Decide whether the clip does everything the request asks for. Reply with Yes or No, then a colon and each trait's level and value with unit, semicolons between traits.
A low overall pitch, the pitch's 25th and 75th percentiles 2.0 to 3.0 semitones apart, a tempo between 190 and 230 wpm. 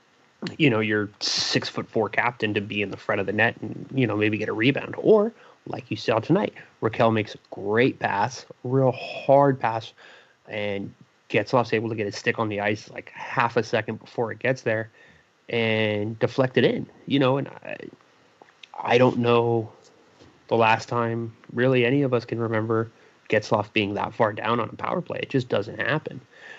Yes: low, 115 Hz; average, 2.7 semitones; average, 195 wpm